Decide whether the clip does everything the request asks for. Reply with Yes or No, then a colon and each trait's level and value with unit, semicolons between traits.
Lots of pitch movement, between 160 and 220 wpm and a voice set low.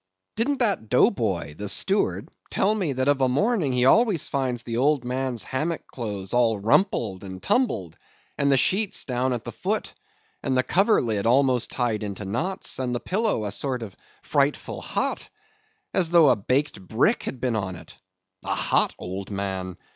Yes: wide, 6.7 semitones; average, 175 wpm; low, 125 Hz